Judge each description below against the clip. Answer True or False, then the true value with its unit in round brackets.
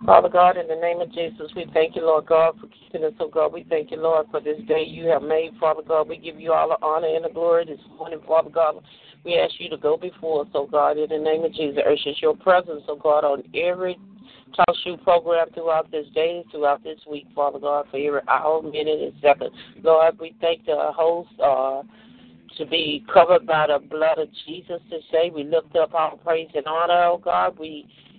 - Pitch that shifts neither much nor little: False (1.9 semitones)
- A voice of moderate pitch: True (160 Hz)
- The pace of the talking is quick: True (225 wpm)